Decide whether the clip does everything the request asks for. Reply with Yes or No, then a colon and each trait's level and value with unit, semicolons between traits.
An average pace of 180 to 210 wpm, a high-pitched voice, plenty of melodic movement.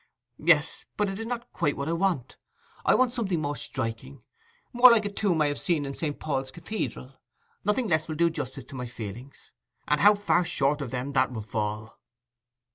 No: average, 195 wpm; medium, 150 Hz; wide, 7.5 semitones